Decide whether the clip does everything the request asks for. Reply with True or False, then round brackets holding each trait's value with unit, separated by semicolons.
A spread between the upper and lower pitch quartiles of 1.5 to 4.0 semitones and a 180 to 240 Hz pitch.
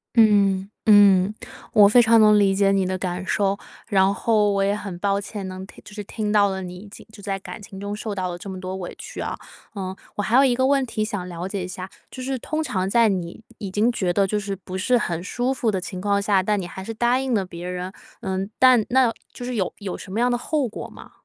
True (2.8 semitones; 200 Hz)